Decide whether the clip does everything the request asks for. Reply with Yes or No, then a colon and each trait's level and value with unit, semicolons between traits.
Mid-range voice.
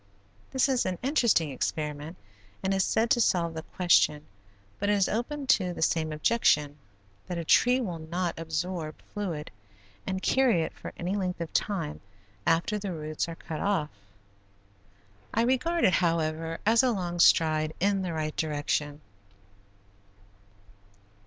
Yes: medium, 175 Hz